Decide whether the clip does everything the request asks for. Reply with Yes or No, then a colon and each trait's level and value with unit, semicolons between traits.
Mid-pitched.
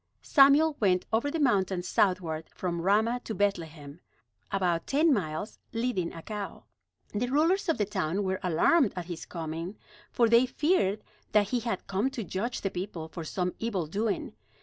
No: high, 200 Hz